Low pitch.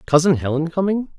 No: medium, 165 Hz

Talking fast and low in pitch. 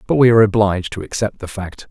Yes: fast, 250 wpm; low, 105 Hz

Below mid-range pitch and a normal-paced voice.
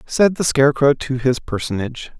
Yes: low, 130 Hz; average, 165 wpm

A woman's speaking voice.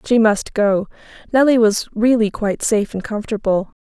Yes: female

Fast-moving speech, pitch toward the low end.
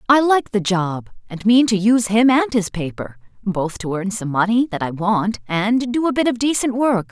No: fast, 230 wpm; high, 215 Hz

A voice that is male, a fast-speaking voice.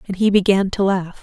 No: female; fast, 245 wpm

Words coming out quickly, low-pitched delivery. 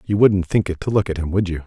Yes: fast, 360 wpm; very low, 95 Hz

